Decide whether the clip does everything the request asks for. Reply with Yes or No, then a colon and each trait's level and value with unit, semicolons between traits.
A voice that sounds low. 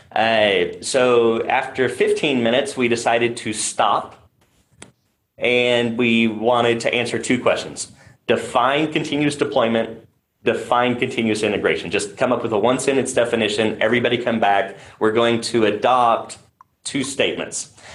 Yes: low, 120 Hz